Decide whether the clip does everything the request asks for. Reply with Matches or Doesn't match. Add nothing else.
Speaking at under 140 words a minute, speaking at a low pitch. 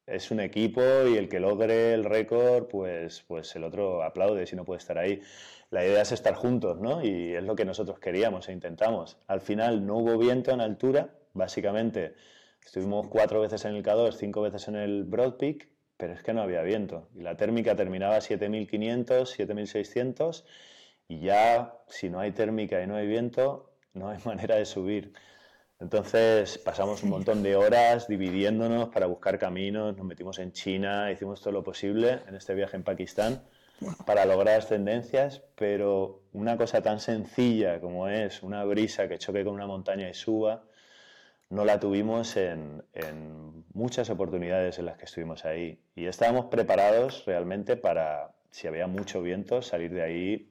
Doesn't match